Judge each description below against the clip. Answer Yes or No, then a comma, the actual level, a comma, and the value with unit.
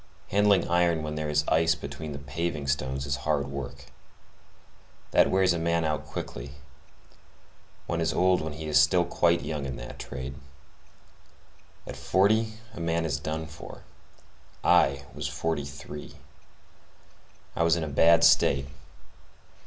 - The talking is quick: No, average, 145 wpm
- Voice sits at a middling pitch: No, very low, 80 Hz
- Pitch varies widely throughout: No, average, 3.2 semitones